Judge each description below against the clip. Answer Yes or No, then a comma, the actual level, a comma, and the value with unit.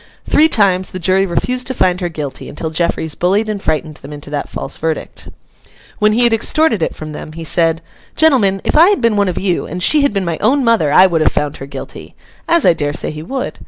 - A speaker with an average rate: No, fast, 235 wpm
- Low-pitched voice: No, medium, 185 Hz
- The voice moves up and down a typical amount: No, wide, 6.1 semitones